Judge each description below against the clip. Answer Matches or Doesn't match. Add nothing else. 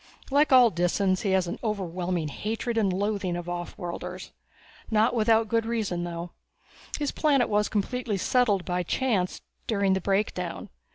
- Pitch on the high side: Matches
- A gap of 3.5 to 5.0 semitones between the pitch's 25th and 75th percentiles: Matches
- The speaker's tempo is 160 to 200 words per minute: Doesn't match